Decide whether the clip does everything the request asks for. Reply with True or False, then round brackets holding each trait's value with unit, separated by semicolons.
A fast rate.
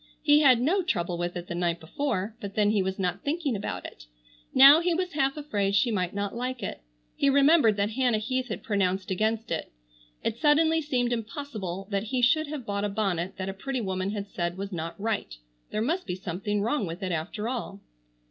True (215 wpm)